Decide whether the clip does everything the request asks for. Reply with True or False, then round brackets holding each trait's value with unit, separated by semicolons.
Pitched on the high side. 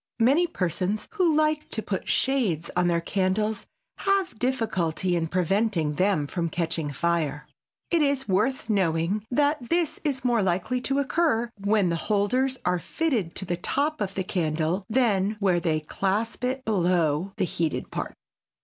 True (200 Hz)